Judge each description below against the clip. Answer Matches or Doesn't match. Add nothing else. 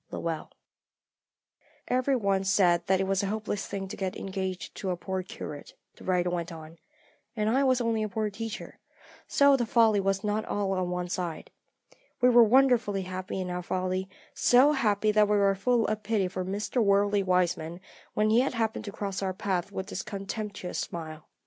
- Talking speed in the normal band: Matches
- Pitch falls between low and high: Doesn't match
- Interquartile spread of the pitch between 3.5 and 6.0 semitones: Doesn't match